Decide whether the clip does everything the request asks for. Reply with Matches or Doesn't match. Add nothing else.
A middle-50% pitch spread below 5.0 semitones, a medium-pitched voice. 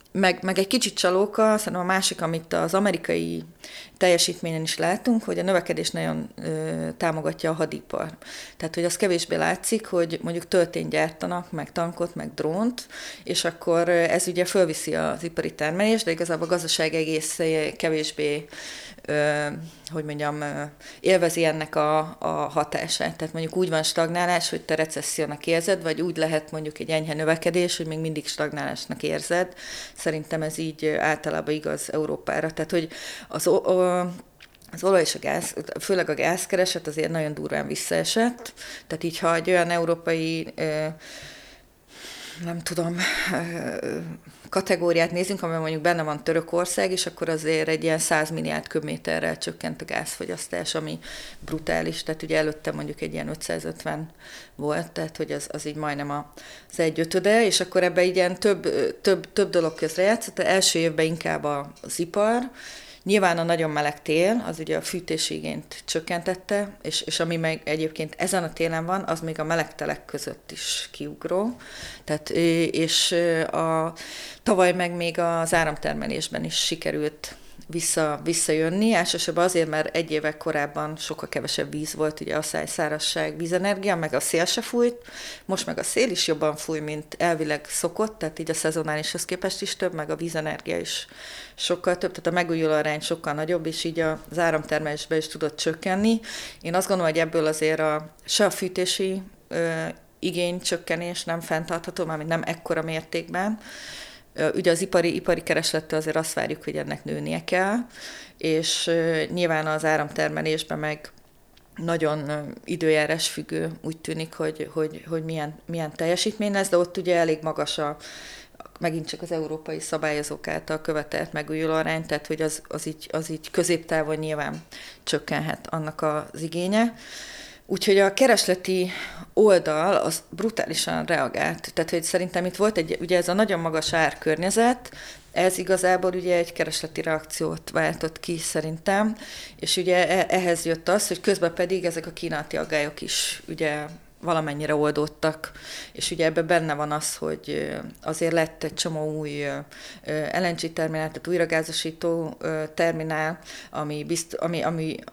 Matches